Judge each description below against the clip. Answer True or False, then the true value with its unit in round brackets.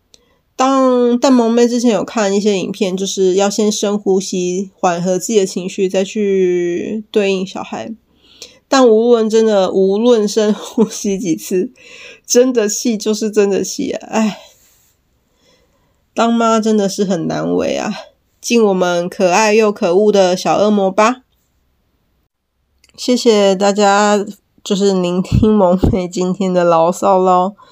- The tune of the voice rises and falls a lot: False (2.9 semitones)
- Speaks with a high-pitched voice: True (205 Hz)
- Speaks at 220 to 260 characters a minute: False (200 characters per minute)